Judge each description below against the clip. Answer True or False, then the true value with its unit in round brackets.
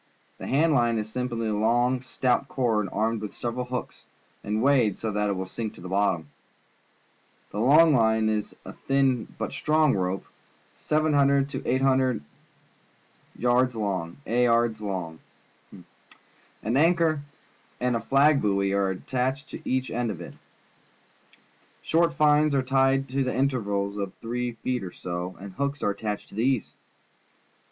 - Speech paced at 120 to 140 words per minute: False (150 wpm)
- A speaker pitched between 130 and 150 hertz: False (120 Hz)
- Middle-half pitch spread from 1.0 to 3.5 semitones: False (4.5 semitones)